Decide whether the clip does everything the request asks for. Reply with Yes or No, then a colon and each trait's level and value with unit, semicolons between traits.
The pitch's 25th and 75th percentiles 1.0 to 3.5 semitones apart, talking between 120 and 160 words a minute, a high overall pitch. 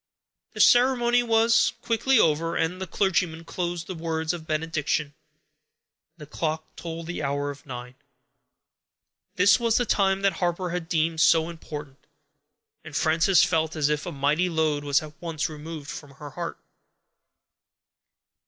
No: average, 3.2 semitones; average, 150 wpm; medium, 165 Hz